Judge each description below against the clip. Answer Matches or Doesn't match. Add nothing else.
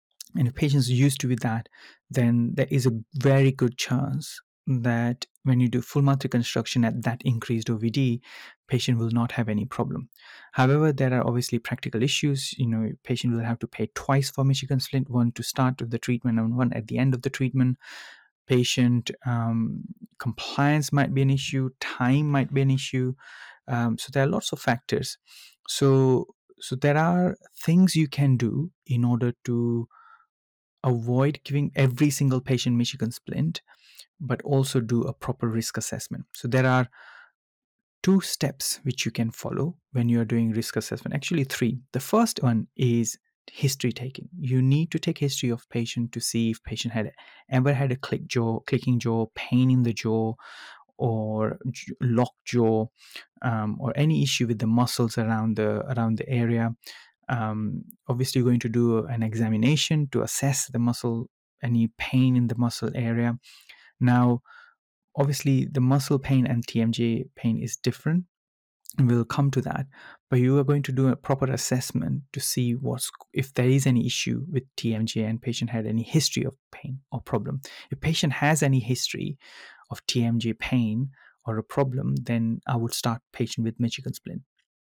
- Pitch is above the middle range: Doesn't match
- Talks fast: Doesn't match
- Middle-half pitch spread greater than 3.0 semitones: Doesn't match